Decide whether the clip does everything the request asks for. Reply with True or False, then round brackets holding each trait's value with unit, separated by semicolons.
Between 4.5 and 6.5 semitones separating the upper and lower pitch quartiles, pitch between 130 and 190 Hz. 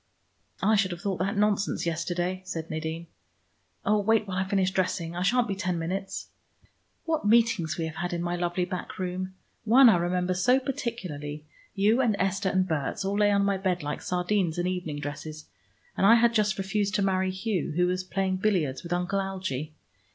False (2.5 semitones; 185 Hz)